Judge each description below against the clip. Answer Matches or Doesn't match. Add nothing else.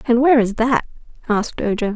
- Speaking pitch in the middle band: Doesn't match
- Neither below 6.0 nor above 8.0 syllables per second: Matches